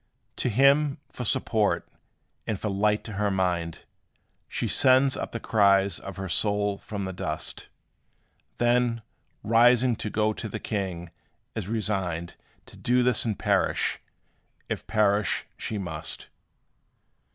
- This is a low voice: Yes, low, 105 Hz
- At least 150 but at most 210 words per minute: No, slow, 135 wpm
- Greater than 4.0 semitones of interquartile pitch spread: No, average, 3.2 semitones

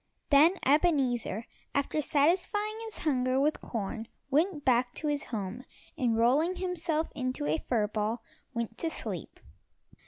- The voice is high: Yes, very high, 270 Hz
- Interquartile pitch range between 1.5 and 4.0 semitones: No, average, 5.3 semitones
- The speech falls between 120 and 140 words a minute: Yes, slow, 135 wpm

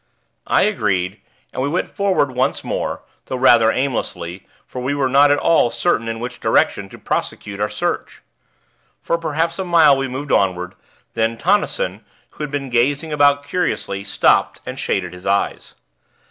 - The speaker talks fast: No, average, 165 wpm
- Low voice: Yes, low, 130 Hz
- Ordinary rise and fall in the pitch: No, wide, 5.7 semitones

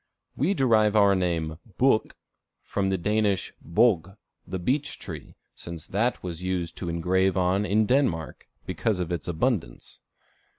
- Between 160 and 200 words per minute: No, average, 140 wpm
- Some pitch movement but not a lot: Yes, average, 4.1 semitones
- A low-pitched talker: Yes, very low, 95 Hz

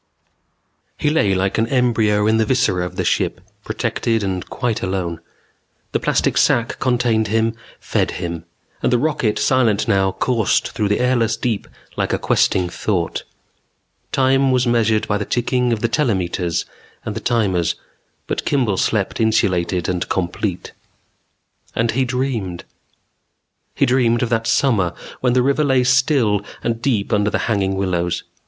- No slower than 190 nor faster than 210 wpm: No, average, 155 wpm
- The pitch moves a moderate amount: Yes, average, 4.4 semitones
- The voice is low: Yes, low, 110 Hz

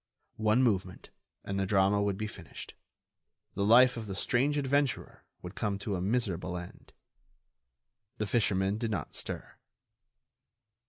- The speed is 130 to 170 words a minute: Yes, average, 140 wpm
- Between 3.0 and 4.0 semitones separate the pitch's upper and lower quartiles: Yes, average, 3.4 semitones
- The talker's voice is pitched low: Yes, low, 105 Hz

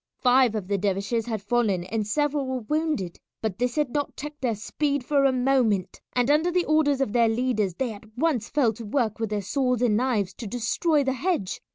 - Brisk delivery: Yes, fast, 215 wpm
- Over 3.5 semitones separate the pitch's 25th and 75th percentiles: Yes, average, 4.8 semitones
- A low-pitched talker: No, high, 245 Hz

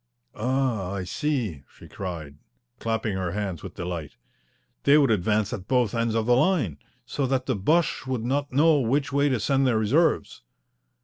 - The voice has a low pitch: Yes, low, 115 Hz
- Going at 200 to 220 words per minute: No, average, 175 wpm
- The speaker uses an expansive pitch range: Yes, wide, 5.8 semitones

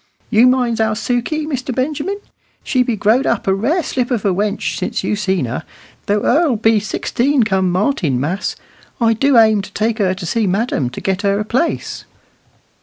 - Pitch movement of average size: Yes, average, 4.2 semitones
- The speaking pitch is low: No, high, 220 Hz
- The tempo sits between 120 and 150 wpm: No, average, 180 wpm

